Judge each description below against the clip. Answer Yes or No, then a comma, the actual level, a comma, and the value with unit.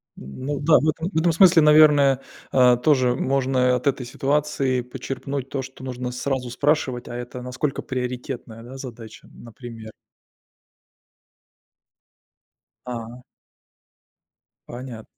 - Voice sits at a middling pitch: No, low, 130 Hz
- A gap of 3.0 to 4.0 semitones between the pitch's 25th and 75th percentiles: No, narrow, 2.4 semitones